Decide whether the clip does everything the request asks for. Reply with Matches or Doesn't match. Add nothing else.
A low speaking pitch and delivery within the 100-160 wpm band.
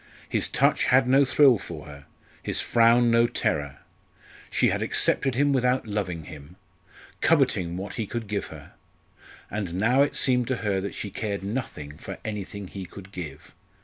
Doesn't match